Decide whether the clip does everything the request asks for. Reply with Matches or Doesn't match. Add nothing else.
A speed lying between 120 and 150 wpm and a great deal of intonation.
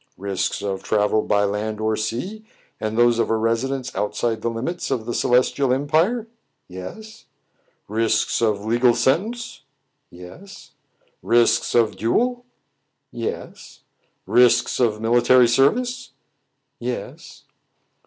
Doesn't match